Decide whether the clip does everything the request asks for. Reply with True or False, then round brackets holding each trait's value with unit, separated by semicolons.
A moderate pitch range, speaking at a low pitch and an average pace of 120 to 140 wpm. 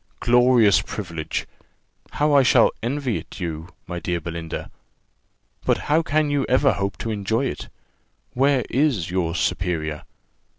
False (7.6 semitones; 110 Hz; 135 wpm)